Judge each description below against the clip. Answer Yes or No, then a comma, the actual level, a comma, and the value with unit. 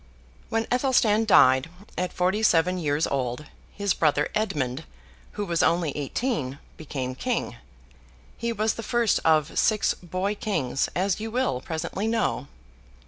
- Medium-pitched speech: Yes, medium, 180 Hz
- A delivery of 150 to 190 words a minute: No, average, 140 wpm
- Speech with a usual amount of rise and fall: No, wide, 6.8 semitones